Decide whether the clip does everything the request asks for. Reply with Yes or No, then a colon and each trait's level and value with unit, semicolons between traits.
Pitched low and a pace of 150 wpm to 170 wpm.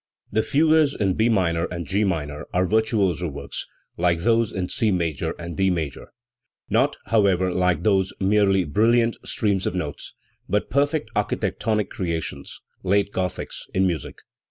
Yes: very low, 95 Hz; average, 155 wpm